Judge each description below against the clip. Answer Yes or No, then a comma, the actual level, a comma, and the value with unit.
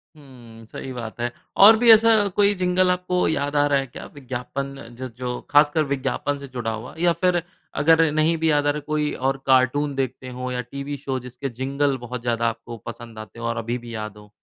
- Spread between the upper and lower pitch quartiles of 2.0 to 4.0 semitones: Yes, average, 3.7 semitones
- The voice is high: No, low, 135 Hz